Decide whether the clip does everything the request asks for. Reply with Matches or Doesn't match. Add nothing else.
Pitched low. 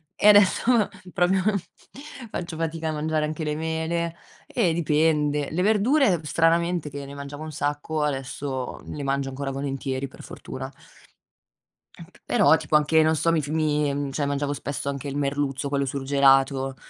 Doesn't match